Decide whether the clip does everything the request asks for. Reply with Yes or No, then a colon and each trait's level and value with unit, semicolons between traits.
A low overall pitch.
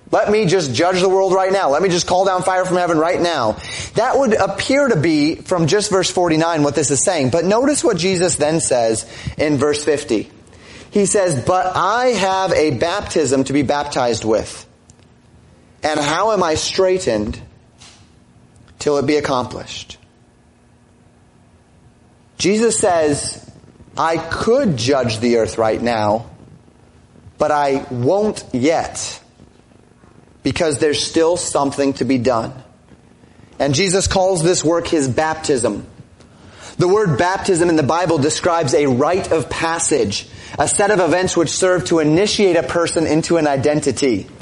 No: medium, 165 Hz